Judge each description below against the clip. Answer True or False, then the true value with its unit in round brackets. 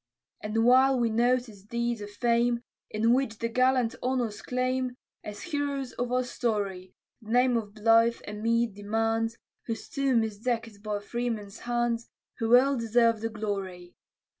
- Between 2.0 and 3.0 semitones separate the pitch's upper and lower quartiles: True (2.5 semitones)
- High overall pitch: True (230 Hz)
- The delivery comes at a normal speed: True (155 wpm)